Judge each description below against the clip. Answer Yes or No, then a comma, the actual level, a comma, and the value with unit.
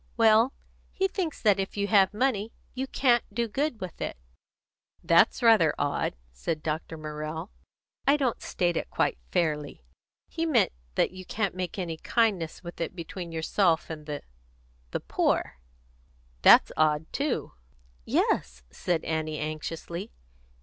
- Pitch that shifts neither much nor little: No, wide, 6.1 semitones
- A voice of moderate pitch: Yes, medium, 180 Hz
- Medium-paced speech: Yes, average, 145 wpm